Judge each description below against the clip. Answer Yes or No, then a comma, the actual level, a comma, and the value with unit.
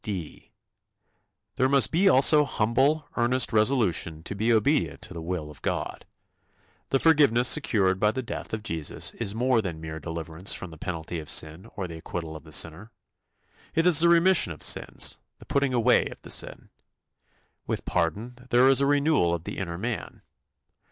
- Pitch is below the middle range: Yes, low, 110 Hz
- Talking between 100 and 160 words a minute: No, average, 180 wpm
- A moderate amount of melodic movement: No, wide, 7.9 semitones